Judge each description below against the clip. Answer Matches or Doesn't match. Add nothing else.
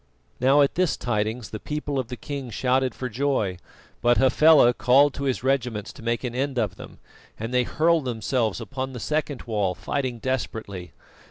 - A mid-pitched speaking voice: Doesn't match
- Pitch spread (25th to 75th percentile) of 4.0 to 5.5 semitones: Doesn't match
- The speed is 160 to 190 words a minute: Matches